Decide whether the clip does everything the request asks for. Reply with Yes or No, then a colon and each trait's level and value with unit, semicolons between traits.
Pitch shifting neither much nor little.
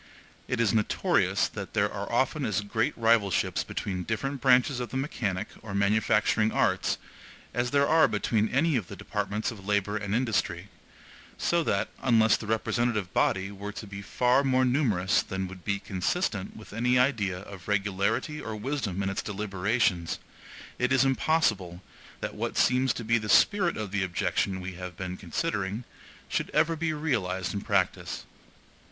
Yes: average, 4.5 semitones